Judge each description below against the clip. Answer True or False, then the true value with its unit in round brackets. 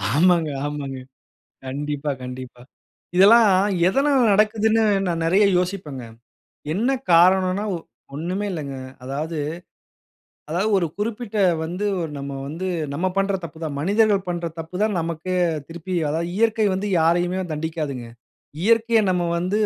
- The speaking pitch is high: False (175 Hz)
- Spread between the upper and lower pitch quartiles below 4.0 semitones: False (4.7 semitones)